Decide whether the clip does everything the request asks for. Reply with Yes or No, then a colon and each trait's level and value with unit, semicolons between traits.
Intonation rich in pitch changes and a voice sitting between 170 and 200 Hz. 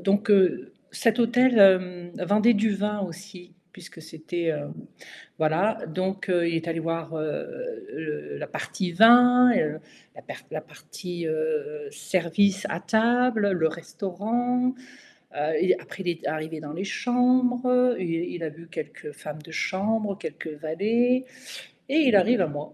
Yes: wide, 6.4 semitones; high, 190 Hz